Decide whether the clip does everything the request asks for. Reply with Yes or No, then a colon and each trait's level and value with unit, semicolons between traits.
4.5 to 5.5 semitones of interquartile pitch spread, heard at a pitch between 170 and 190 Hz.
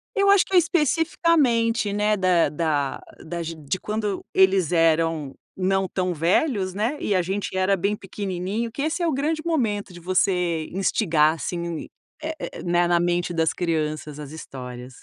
Yes: average, 4.8 semitones; medium, 185 Hz